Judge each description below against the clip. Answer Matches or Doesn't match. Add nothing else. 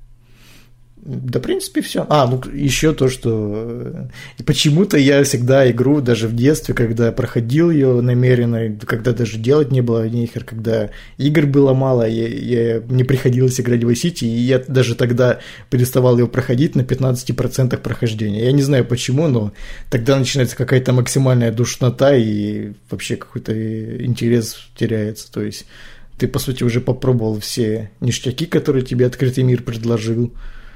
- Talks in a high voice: Doesn't match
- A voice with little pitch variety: Matches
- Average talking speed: Matches